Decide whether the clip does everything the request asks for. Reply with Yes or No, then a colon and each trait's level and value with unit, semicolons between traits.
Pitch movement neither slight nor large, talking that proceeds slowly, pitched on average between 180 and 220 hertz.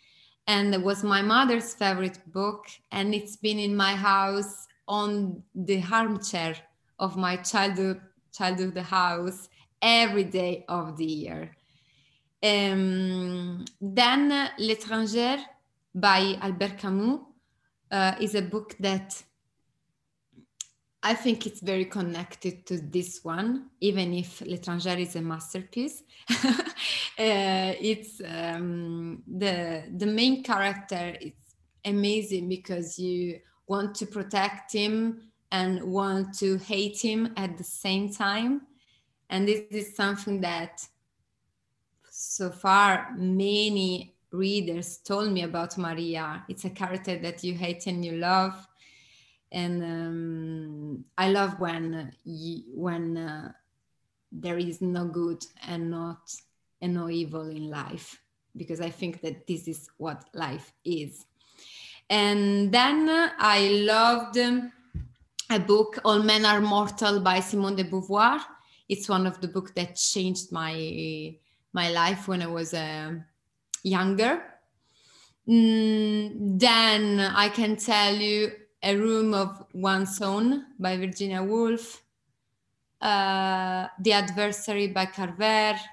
Yes: average, 3.3 semitones; slow, 120 wpm; high, 190 Hz